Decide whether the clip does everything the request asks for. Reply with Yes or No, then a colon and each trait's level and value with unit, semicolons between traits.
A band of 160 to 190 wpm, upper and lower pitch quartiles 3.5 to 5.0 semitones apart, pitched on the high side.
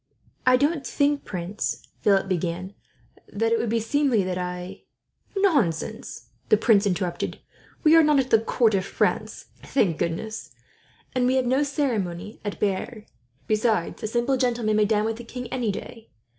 Yes: average, 170 wpm; average, 4.6 semitones; high, 220 Hz